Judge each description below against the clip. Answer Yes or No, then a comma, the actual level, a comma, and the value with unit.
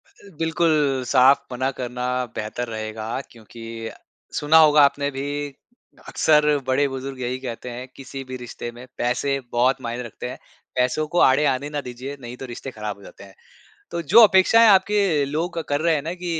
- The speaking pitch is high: No, low, 130 Hz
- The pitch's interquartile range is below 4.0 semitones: Yes, average, 3.6 semitones